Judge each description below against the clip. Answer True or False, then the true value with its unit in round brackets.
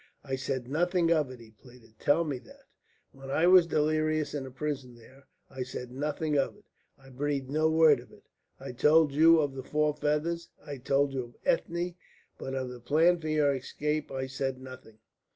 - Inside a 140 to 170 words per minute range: False (200 wpm)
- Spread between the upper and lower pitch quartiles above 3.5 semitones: False (3.0 semitones)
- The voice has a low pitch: False (145 Hz)